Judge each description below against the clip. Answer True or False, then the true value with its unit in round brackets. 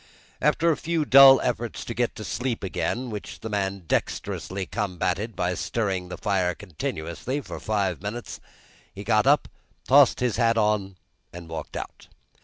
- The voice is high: False (105 Hz)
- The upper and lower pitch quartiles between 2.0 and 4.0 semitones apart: False (4.5 semitones)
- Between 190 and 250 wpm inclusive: False (160 wpm)